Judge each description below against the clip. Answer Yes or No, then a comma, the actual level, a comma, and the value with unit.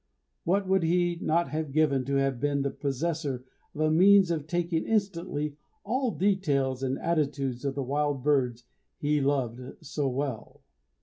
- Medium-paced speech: Yes, average, 165 wpm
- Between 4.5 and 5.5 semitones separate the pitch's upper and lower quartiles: No, average, 3.9 semitones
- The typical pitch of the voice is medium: Yes, medium, 145 Hz